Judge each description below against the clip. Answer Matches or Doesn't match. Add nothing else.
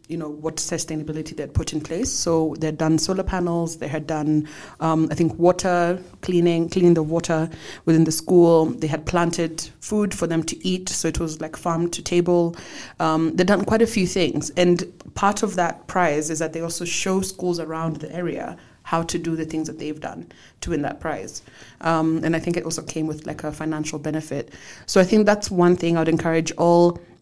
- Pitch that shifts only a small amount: Matches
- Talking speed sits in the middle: Doesn't match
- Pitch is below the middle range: Doesn't match